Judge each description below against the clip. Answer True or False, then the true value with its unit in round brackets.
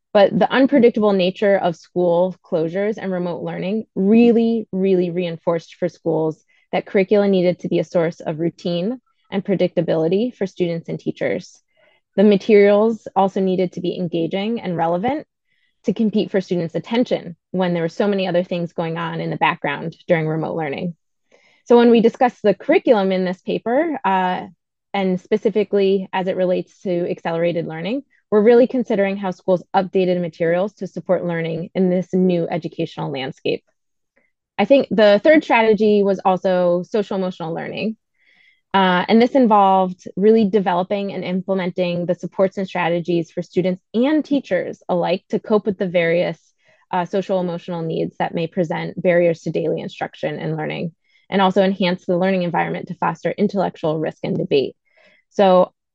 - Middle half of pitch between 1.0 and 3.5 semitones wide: True (3.1 semitones)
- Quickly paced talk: False (160 wpm)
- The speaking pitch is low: False (185 Hz)